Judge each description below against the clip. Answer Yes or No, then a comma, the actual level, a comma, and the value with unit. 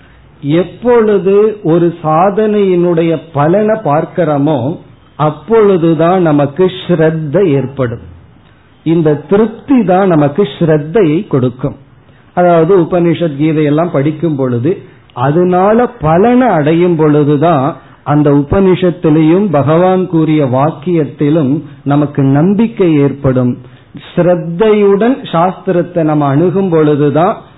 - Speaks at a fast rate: No, average, 80 wpm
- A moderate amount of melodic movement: Yes, average, 4.0 semitones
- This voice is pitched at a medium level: Yes, medium, 160 Hz